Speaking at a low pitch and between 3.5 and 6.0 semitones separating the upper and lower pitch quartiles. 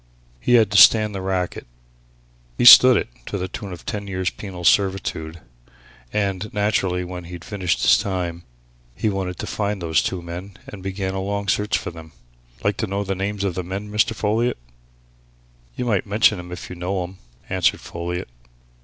No: very low, 95 Hz; narrow, 2.4 semitones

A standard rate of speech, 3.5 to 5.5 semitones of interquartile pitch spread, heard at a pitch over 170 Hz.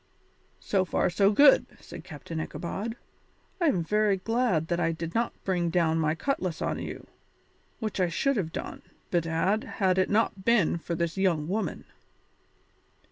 Yes: average, 160 wpm; average, 4.2 semitones; medium, 185 Hz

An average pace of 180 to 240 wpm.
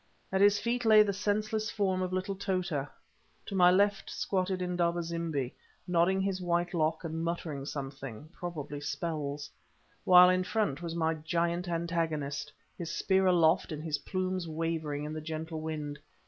No: average, 155 wpm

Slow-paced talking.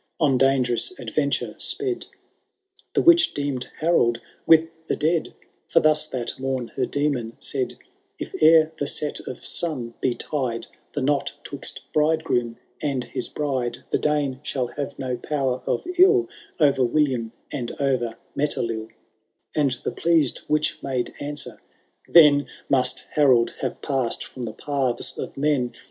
No: average, 150 wpm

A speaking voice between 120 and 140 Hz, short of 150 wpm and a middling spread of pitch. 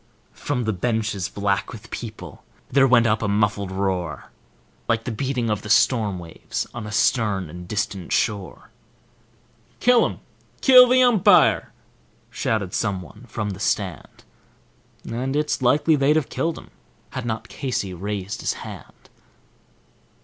No: low, 110 Hz; average, 140 wpm; average, 4.3 semitones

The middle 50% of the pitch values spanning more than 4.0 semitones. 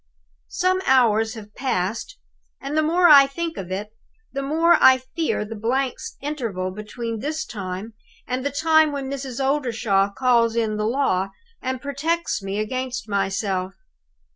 Yes: average, 5.1 semitones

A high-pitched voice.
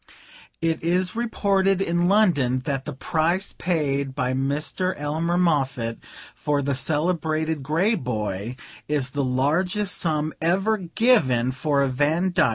No: medium, 155 Hz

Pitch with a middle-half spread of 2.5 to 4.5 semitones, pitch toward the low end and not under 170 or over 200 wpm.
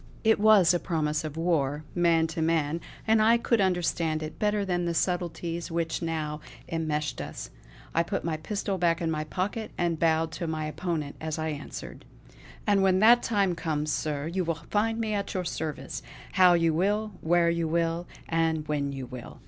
No: average, 2.9 semitones; medium, 165 Hz; average, 190 wpm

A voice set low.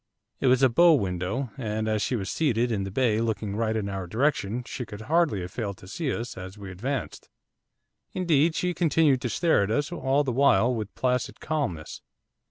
Yes: low, 120 Hz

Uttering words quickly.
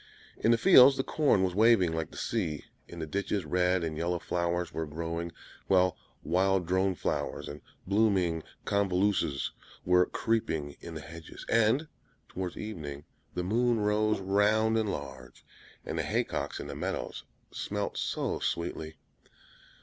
No: average, 150 wpm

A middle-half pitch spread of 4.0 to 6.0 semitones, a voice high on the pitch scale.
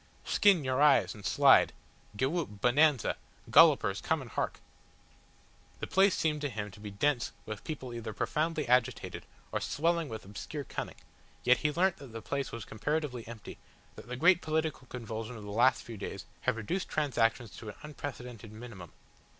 No: average, 5.3 semitones; low, 125 Hz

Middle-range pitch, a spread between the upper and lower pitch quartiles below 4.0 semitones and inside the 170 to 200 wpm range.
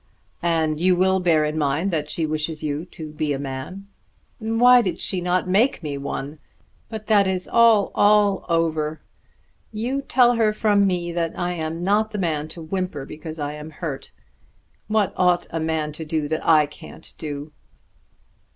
No: medium, 170 Hz; average, 4.4 semitones; average, 175 wpm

